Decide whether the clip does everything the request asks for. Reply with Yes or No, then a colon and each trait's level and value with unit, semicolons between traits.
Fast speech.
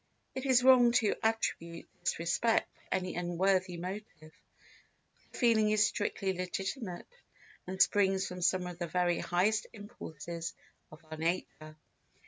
No: average, 140 wpm